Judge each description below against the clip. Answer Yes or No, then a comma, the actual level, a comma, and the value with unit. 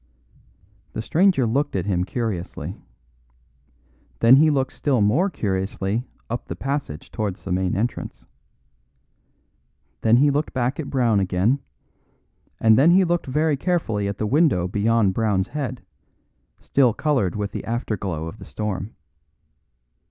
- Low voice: Yes, low, 115 Hz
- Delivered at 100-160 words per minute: Yes, average, 140 wpm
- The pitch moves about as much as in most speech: No, wide, 5.9 semitones